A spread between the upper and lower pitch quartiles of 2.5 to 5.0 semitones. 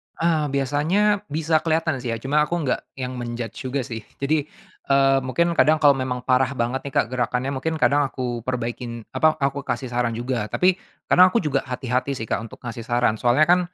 Yes: average, 3.7 semitones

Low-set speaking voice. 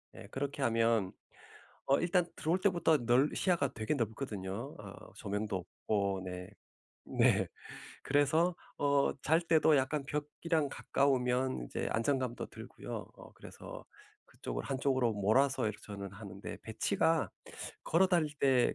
Yes: low, 130 Hz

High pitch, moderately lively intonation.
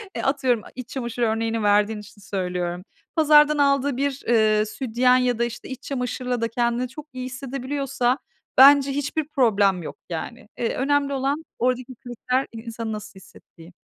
Yes: very high, 250 Hz; average, 3.7 semitones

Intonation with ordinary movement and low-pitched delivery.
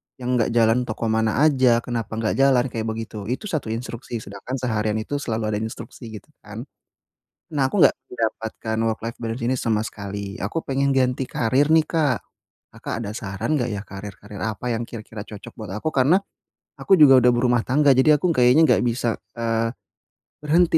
Yes: average, 3.3 semitones; low, 115 Hz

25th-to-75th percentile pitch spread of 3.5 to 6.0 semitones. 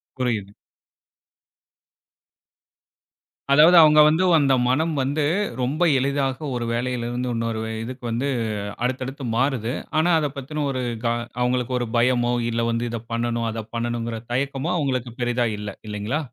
No: average, 2.9 semitones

